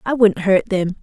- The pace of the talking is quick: Yes, fast, 235 wpm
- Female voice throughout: Yes, female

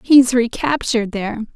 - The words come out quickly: No, slow, 115 wpm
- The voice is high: Yes, high, 240 Hz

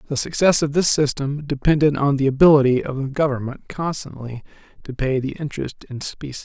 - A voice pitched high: No, medium, 140 Hz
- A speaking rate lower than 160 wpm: No, average, 175 wpm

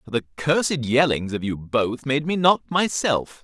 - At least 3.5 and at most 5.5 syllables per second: Yes, 4.5 syllables/s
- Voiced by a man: Yes, male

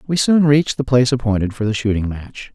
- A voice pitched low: Yes, low, 125 Hz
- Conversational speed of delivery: No, fast, 235 wpm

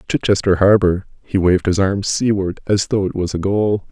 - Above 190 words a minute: Yes, average, 200 wpm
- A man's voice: Yes, male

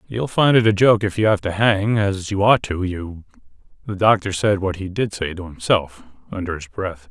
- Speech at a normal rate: No, fast, 230 wpm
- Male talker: Yes, male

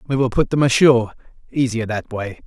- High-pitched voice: No, low, 120 Hz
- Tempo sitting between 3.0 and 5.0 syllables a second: No, 5.9 syllables/s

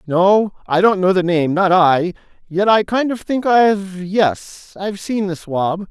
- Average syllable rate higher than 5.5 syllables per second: No, 4.0 syllables/s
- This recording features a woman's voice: No, male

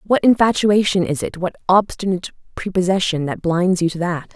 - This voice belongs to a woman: Yes, female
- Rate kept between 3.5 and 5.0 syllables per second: No, 5.5 syllables/s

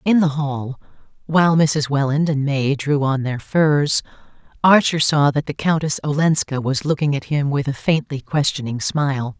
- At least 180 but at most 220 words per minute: No, average, 170 wpm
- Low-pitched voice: No, medium, 145 Hz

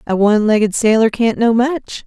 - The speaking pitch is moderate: No, high, 225 Hz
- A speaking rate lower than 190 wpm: No, fast, 205 wpm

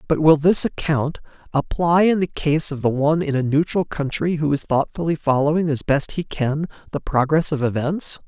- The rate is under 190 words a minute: No, average, 195 wpm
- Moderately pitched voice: Yes, medium, 150 Hz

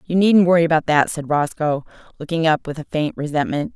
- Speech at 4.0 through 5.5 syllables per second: No, 5.8 syllables/s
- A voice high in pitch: No, medium, 160 Hz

